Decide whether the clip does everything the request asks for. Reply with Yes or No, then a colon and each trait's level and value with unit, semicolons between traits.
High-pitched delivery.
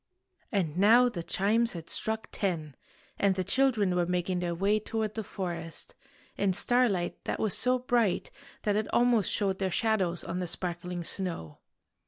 Yes: high, 195 Hz